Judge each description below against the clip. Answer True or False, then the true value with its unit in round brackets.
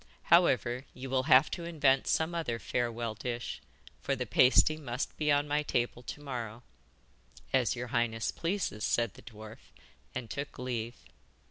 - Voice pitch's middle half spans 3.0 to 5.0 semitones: True (3.7 semitones)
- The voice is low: True (125 Hz)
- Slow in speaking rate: False (155 wpm)